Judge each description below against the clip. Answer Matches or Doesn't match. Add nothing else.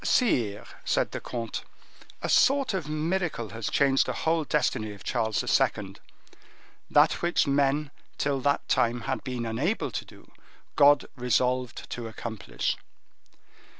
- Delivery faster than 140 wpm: Doesn't match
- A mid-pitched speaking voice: Doesn't match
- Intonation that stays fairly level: Doesn't match